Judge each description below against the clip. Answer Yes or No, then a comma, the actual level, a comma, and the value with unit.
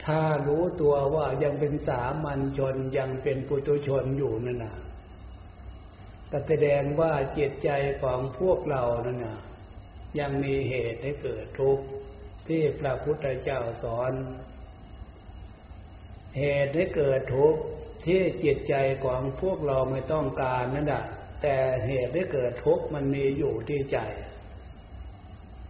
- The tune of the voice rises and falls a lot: Yes, wide, 6.1 semitones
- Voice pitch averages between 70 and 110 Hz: No, low, 130 Hz